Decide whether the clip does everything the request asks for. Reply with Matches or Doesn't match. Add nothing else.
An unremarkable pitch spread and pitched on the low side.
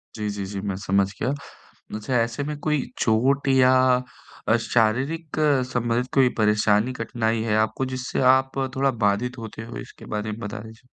Matches